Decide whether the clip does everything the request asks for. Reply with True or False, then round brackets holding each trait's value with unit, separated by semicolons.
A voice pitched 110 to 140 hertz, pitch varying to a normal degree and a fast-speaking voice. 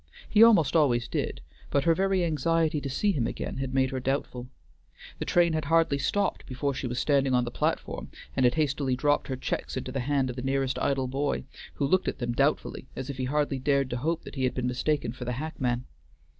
True (135 Hz; 3.1 semitones; 225 wpm)